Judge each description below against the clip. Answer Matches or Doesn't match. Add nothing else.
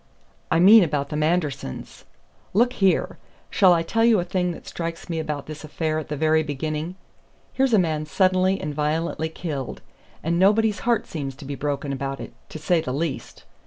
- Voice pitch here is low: Doesn't match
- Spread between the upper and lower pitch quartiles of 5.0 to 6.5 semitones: Doesn't match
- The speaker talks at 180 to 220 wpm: Matches